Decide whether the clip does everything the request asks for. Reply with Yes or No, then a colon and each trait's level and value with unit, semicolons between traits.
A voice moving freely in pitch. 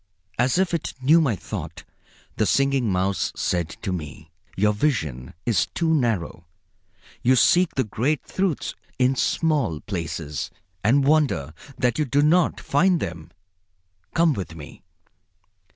Yes: wide, 9.0 semitones